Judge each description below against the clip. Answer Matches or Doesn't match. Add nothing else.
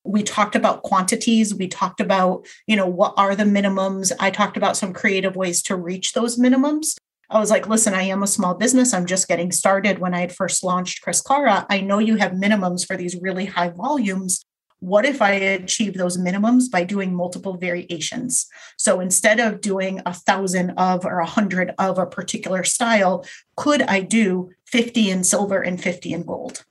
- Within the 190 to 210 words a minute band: Matches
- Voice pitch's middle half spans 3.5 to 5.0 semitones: Doesn't match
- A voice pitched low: Doesn't match